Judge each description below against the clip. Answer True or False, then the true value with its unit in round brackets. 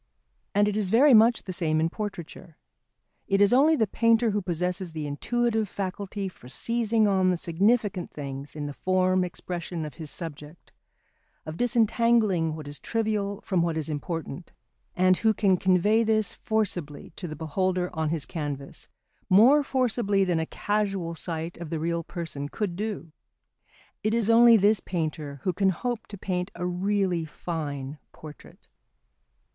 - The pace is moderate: True (160 wpm)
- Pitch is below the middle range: False (185 Hz)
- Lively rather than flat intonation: False (4.7 semitones)